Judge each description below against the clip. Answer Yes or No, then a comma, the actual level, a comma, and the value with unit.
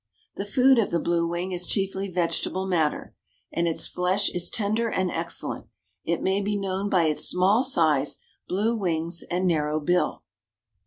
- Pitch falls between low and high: Yes, medium, 180 Hz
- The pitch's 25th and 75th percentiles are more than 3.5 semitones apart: No, average, 2.8 semitones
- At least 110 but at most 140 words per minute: No, average, 165 wpm